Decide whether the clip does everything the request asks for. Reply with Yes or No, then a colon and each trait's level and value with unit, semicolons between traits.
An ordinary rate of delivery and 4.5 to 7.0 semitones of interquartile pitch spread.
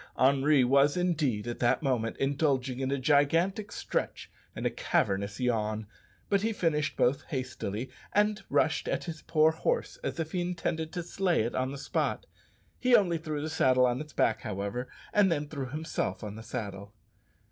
Yes: average, 180 wpm; average, 5.1 semitones